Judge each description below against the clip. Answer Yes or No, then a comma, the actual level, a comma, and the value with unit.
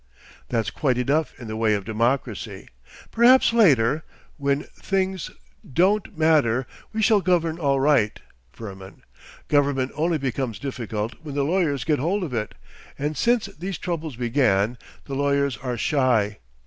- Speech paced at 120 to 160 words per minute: Yes, average, 140 wpm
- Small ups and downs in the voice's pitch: No, wide, 5.5 semitones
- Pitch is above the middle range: No, medium, 140 Hz